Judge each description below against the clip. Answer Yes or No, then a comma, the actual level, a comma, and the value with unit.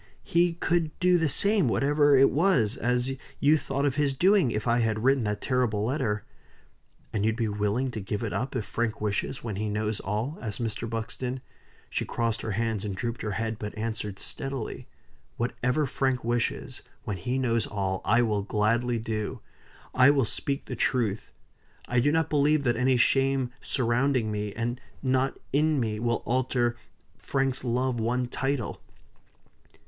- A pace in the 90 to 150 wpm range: No, average, 170 wpm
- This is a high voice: No, low, 120 Hz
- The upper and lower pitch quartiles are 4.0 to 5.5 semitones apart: No, average, 3.6 semitones